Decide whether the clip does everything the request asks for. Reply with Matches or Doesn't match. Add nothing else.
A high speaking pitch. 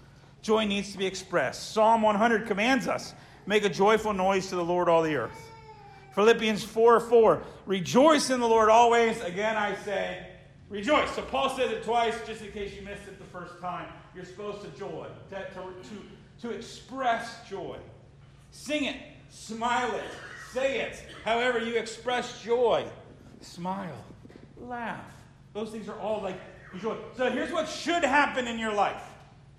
Matches